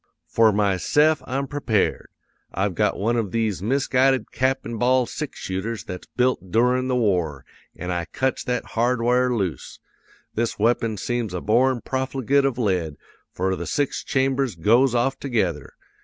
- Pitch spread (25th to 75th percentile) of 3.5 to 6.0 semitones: Yes, average, 4.5 semitones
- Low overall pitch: Yes, low, 120 Hz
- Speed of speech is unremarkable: Yes, average, 155 wpm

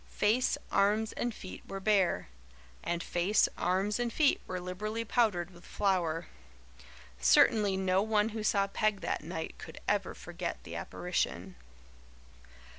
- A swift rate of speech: No, slow, 135 wpm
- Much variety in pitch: No, average, 2.9 semitones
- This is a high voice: Yes, high, 200 Hz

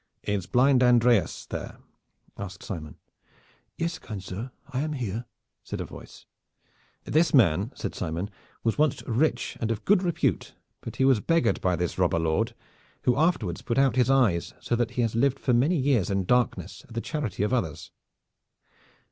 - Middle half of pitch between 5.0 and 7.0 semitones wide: Yes, wide, 5.4 semitones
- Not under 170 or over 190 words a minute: Yes, average, 175 wpm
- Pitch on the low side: Yes, low, 120 Hz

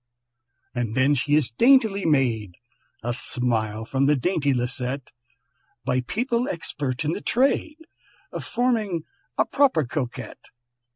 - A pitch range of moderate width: No, wide, 9.0 semitones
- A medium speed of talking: No, slow, 125 wpm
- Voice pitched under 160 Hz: Yes, medium, 140 Hz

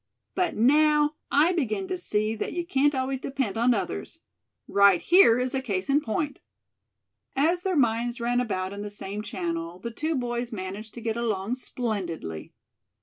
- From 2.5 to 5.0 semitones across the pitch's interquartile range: No, wide, 5.6 semitones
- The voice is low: No, high, 235 Hz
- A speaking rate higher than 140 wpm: Yes, average, 170 wpm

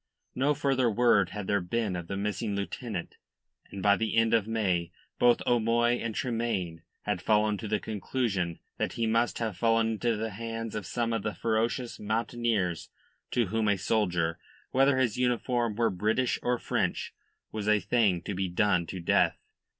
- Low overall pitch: Yes, low, 110 Hz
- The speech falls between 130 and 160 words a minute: No, average, 175 wpm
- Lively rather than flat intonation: No, average, 2.9 semitones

